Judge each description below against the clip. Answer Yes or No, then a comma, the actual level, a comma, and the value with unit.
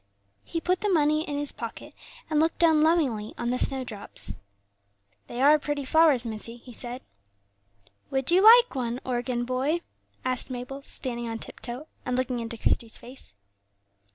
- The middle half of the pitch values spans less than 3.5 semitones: No, average, 4.2 semitones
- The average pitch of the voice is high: Yes, very high, 260 Hz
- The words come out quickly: No, average, 160 wpm